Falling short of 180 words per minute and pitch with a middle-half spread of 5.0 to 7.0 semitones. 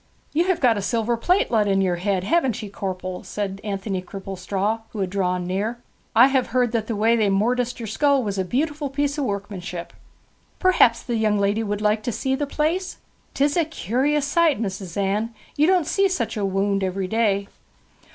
No: average, 200 wpm; wide, 5.4 semitones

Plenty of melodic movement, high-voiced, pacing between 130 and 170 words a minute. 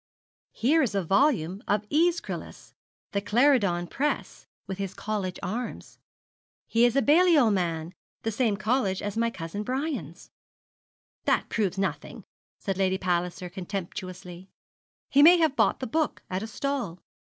Yes: wide, 6.1 semitones; high, 205 Hz; average, 140 wpm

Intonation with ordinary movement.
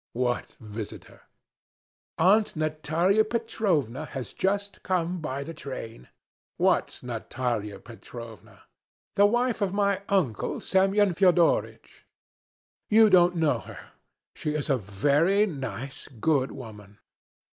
No: wide, 8.0 semitones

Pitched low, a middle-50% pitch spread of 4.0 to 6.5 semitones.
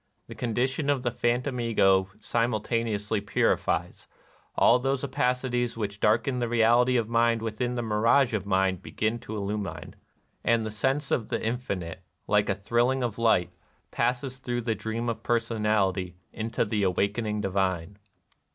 No: low, 115 Hz; average, 2.8 semitones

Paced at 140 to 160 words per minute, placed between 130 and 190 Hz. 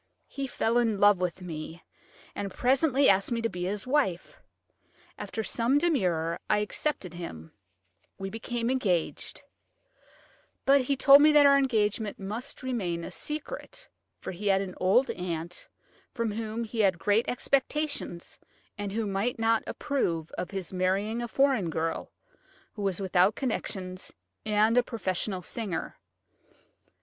No: average, 145 wpm; high, 210 Hz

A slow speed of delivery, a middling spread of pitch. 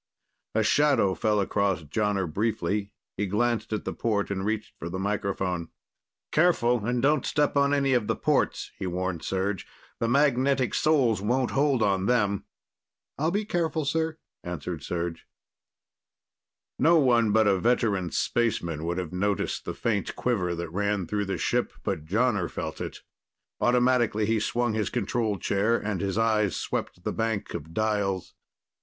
No: average, 160 wpm; average, 4.2 semitones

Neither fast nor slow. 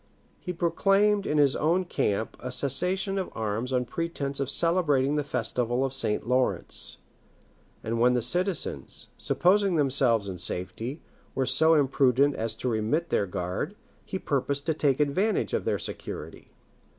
Yes: average, 150 wpm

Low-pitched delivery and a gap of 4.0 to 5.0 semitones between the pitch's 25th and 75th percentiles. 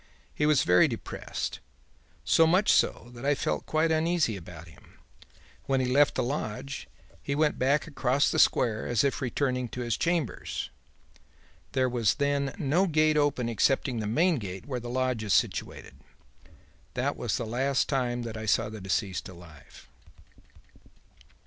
Yes: low, 130 Hz; average, 4.6 semitones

